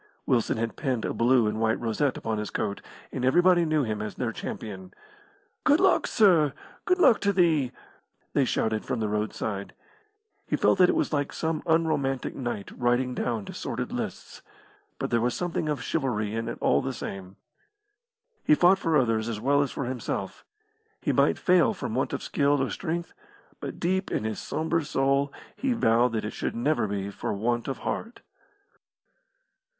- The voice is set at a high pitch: No, low, 130 Hz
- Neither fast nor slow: Yes, average, 180 wpm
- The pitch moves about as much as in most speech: No, wide, 6.2 semitones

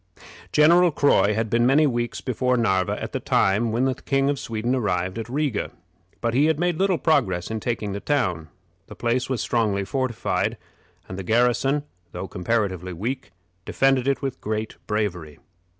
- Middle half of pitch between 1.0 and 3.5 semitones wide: No, average, 4.9 semitones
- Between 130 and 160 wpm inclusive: No, average, 170 wpm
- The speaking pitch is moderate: No, low, 120 Hz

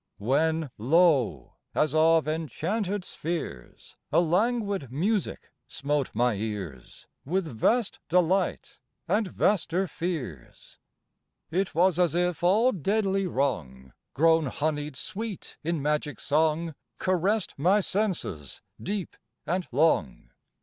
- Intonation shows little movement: No, average, 5.0 semitones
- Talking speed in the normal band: No, slow, 110 wpm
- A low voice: No, medium, 165 Hz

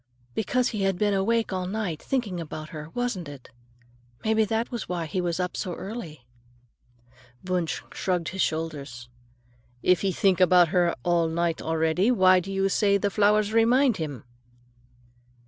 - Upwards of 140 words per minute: Yes, average, 160 wpm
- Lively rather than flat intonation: No, average, 4.2 semitones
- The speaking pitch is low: No, medium, 185 Hz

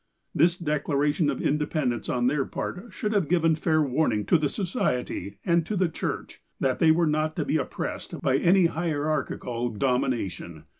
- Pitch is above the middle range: No, medium, 150 Hz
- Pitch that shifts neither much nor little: Yes, average, 4.5 semitones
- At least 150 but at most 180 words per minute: Yes, average, 170 wpm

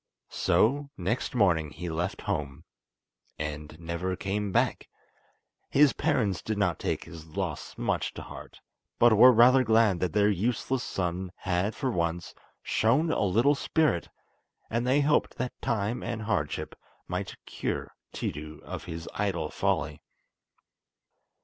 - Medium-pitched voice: No, low, 100 Hz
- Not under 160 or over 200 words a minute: No, slow, 135 wpm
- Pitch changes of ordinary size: No, wide, 6.1 semitones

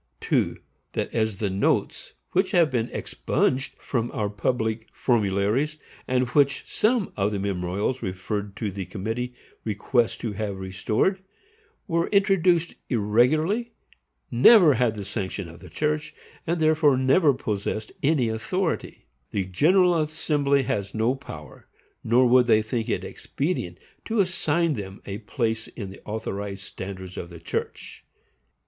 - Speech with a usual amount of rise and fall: No, wide, 6.9 semitones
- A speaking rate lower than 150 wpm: Yes, average, 140 wpm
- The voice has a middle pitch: No, low, 115 Hz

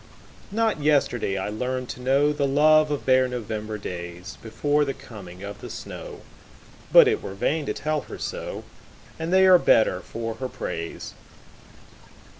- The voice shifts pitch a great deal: Yes, wide, 5.9 semitones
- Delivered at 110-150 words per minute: Yes, average, 140 wpm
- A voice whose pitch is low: Yes, low, 130 Hz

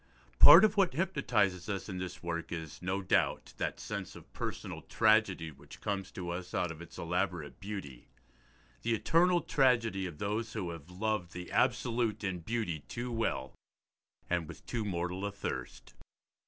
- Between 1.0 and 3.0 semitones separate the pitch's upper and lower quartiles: No, average, 4.7 semitones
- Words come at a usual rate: Yes, average, 165 wpm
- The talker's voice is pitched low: Yes, very low, 95 Hz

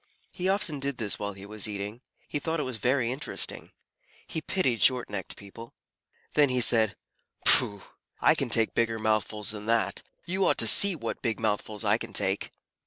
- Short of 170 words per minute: No, average, 180 wpm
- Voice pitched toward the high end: No, low, 115 Hz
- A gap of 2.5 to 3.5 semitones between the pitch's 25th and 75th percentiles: No, average, 4.7 semitones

